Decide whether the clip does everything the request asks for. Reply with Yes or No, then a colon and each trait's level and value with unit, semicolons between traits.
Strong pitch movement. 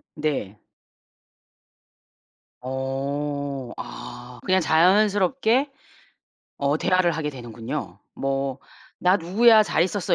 Yes: wide, 5.7 semitones